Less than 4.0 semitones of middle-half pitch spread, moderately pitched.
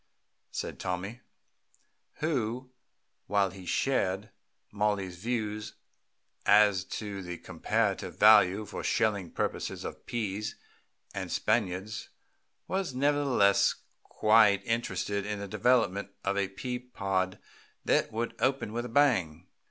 No: average, 3.4 semitones; low, 105 Hz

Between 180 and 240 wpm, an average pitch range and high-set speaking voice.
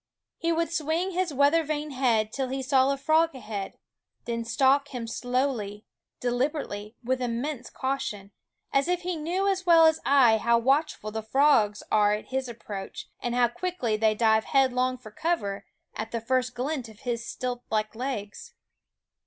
No: average, 170 wpm; average, 4.8 semitones; very high, 255 Hz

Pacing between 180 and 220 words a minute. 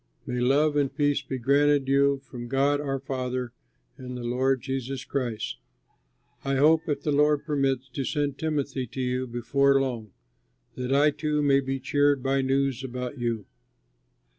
No: average, 165 wpm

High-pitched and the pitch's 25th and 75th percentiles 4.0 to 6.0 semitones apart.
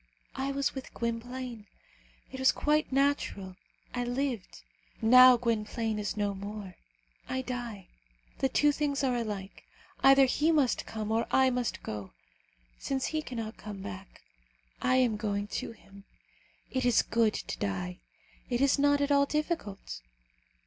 Yes: high, 245 Hz; average, 4.3 semitones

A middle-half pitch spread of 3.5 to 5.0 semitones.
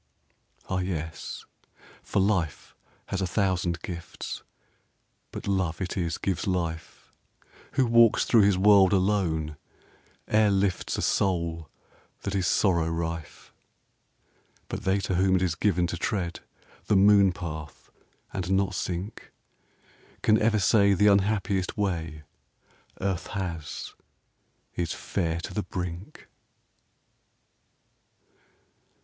No: average, 2.8 semitones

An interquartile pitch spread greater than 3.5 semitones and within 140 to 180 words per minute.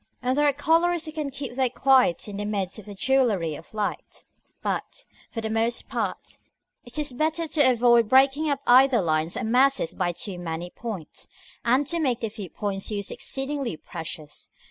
No: wide, 5.5 semitones; average, 190 wpm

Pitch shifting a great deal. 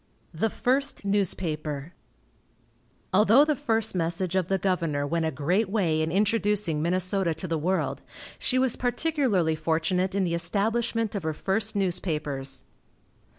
No: average, 4.7 semitones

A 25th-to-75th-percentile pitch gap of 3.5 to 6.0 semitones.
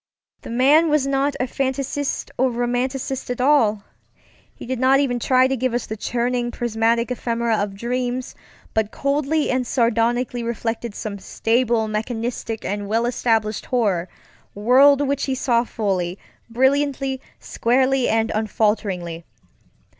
No: average, 2.8 semitones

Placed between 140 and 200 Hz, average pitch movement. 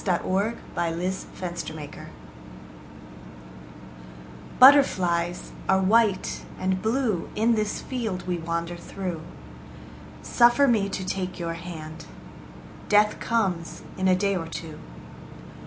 Yes: medium, 185 Hz; average, 3.8 semitones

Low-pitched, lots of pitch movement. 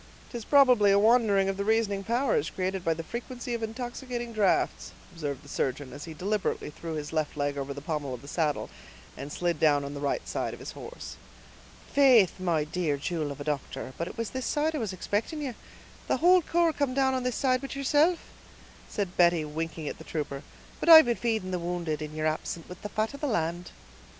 No: high, 190 Hz; wide, 8.0 semitones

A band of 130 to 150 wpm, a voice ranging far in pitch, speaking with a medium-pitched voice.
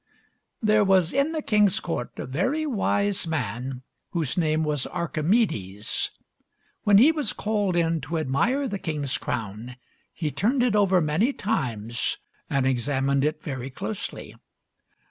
Yes: average, 140 wpm; wide, 7.7 semitones; medium, 165 Hz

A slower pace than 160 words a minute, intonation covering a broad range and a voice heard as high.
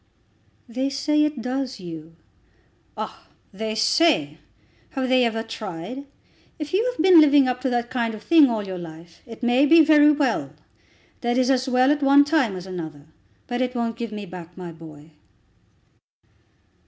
No: average, 170 wpm; wide, 6.9 semitones; high, 245 Hz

